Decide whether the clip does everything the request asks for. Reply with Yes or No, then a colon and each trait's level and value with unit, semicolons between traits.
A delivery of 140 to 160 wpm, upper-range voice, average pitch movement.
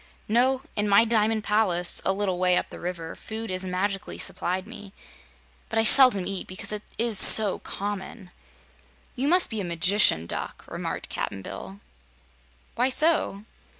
Yes: average, 155 wpm; high, 205 Hz; average, 3.4 semitones